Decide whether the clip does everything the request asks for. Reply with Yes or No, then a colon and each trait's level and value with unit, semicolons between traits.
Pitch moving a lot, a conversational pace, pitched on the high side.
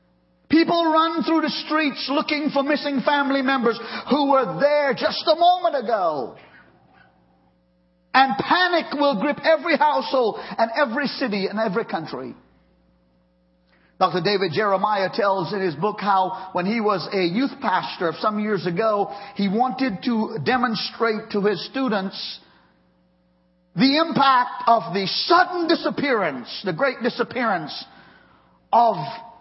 No: wide, 6.7 semitones; slow, 130 wpm; high, 230 Hz